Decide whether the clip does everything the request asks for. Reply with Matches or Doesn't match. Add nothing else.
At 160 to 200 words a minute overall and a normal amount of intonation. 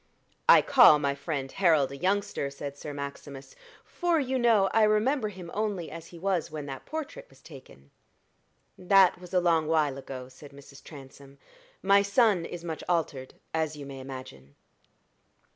Doesn't match